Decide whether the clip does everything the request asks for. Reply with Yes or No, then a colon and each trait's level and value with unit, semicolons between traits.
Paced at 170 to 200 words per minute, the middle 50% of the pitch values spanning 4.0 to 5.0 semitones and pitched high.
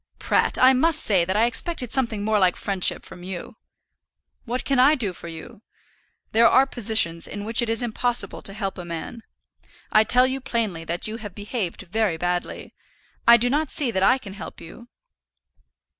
Yes: average, 190 wpm; average, 4.5 semitones; high, 220 Hz